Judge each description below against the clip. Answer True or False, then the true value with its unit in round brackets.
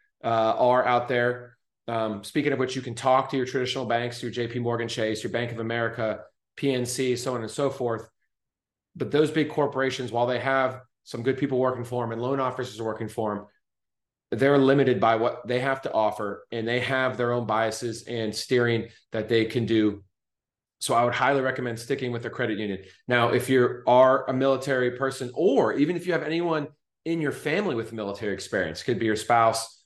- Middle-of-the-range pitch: False (125 Hz)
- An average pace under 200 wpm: False (205 wpm)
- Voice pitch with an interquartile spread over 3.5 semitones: False (2.5 semitones)